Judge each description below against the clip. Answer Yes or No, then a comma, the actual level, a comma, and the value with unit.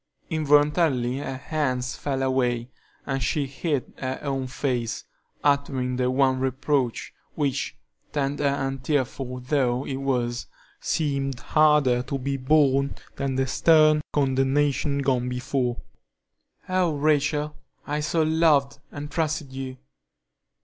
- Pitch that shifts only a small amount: Yes, narrow, 2.3 semitones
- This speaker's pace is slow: Yes, slow, 120 wpm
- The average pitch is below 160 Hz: Yes, low, 135 Hz